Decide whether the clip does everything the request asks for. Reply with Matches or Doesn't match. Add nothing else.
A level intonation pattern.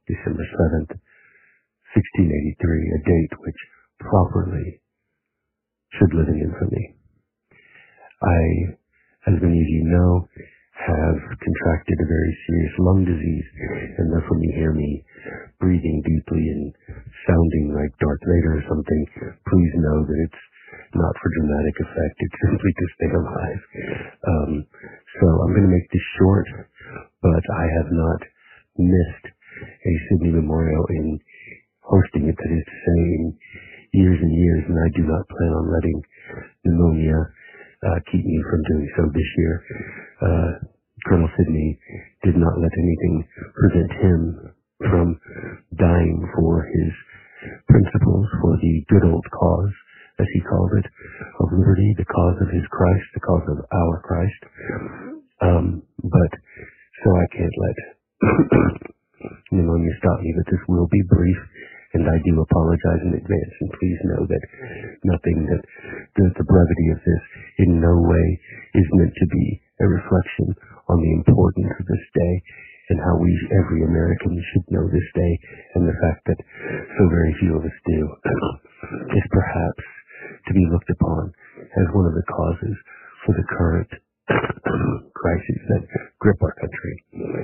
Matches